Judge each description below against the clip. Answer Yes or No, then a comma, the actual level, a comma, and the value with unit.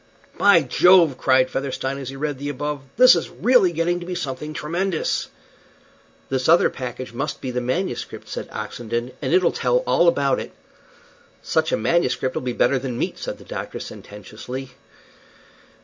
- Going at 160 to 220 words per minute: Yes, average, 165 wpm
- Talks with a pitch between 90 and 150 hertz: Yes, medium, 140 Hz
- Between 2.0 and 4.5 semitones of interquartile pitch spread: No, average, 5.0 semitones